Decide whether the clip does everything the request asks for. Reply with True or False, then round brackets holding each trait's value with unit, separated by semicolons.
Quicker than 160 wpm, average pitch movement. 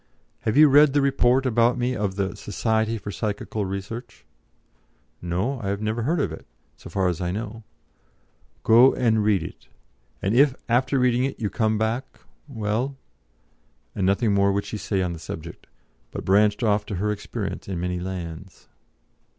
True (170 wpm; 3.9 semitones)